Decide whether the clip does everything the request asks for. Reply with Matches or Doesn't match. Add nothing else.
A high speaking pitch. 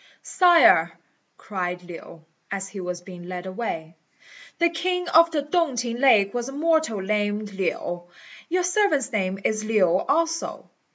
Matches